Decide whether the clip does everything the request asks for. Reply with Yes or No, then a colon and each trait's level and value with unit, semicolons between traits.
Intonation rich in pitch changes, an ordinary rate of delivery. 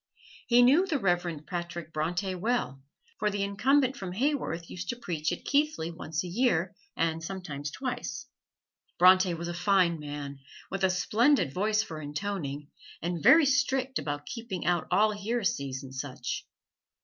Yes: wide, 6.3 semitones; average, 155 wpm